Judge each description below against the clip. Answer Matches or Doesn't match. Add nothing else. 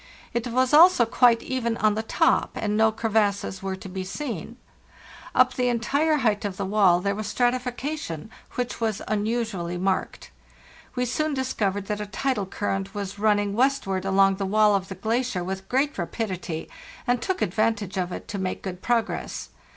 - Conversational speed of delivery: Matches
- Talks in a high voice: Matches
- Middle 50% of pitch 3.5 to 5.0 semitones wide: Matches